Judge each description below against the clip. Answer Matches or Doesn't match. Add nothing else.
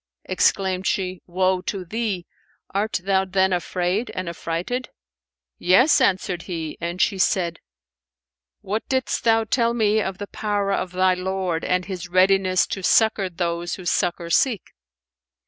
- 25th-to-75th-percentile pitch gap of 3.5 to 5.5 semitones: Doesn't match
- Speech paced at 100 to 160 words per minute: Matches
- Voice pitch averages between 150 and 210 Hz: Matches